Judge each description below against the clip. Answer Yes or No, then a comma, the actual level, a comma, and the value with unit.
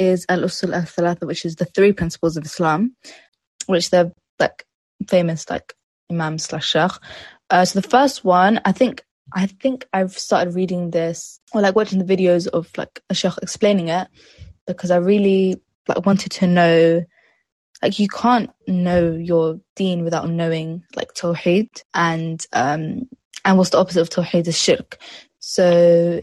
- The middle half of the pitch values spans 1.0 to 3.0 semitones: Yes, narrow, 2.4 semitones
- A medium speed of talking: Yes, average, 160 wpm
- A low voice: No, medium, 180 Hz